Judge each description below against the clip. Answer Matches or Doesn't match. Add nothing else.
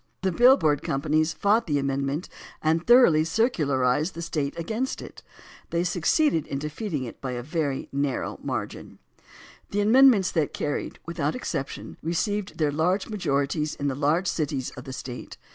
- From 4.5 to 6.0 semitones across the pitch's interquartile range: Matches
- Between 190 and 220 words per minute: Doesn't match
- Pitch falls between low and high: Matches